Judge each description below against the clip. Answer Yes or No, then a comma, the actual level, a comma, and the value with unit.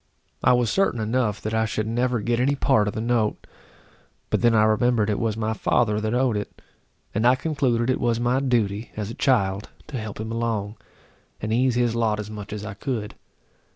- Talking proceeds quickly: Yes, fast, 210 wpm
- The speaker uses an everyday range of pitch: No, narrow, 2.3 semitones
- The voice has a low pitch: Yes, low, 115 Hz